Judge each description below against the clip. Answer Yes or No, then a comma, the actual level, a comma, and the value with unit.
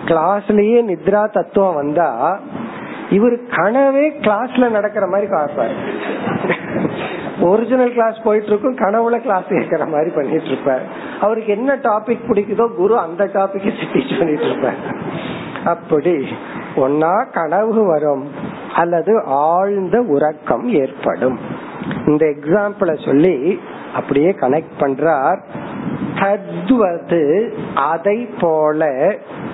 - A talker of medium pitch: No, high, 205 Hz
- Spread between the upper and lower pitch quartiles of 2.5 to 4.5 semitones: No, average, 5.2 semitones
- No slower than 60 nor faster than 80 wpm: No, average, 90 wpm